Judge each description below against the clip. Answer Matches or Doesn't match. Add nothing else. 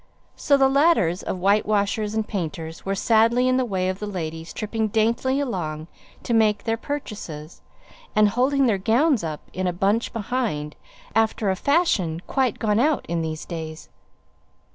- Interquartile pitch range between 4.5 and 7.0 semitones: Matches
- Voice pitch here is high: Matches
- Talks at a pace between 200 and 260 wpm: Doesn't match